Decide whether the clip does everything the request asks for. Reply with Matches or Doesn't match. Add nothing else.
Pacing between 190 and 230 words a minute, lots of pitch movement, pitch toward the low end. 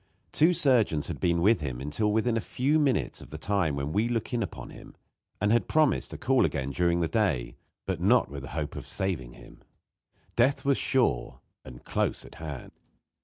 Matches